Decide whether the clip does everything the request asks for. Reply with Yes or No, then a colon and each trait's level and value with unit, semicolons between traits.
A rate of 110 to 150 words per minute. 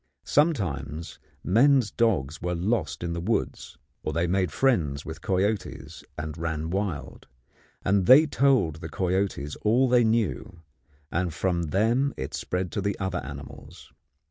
Yes: average, 145 wpm